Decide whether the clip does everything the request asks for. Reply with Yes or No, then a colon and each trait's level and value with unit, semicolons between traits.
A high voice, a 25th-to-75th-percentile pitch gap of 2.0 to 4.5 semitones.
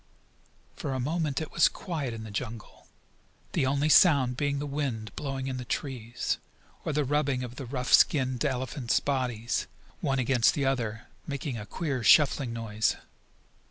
No: low, 130 Hz; average, 3.2 semitones